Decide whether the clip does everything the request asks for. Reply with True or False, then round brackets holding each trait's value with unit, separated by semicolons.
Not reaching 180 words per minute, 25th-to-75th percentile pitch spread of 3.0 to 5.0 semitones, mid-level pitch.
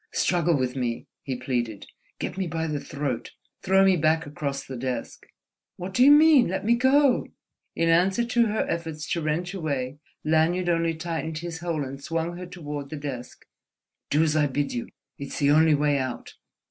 False (185 wpm; 3.9 semitones; 160 Hz)